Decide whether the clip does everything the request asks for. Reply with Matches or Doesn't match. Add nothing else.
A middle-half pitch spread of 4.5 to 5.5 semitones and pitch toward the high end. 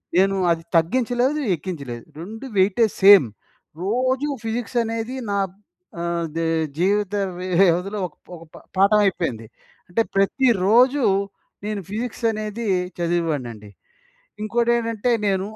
Matches